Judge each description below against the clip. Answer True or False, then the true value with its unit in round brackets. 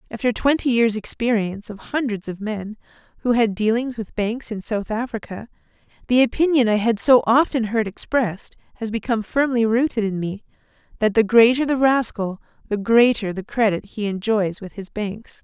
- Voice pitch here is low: False (225 Hz)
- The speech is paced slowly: False (170 wpm)